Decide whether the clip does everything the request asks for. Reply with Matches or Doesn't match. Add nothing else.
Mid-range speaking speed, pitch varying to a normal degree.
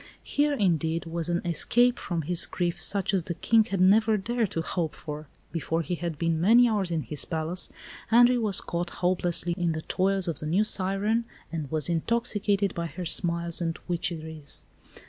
Matches